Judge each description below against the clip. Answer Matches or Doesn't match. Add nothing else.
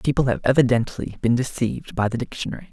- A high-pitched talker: Doesn't match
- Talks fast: Doesn't match